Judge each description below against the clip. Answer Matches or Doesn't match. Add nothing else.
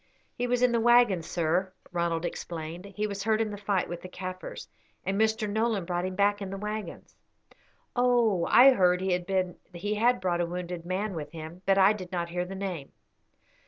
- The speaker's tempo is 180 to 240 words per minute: Matches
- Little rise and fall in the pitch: Doesn't match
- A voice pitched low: Doesn't match